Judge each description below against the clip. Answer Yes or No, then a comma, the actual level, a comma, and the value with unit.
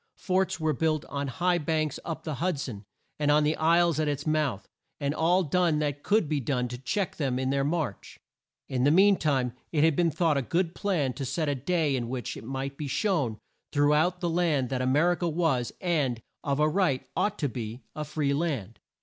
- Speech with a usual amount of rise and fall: Yes, average, 4.1 semitones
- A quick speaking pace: Yes, fast, 225 wpm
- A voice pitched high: No, medium, 150 Hz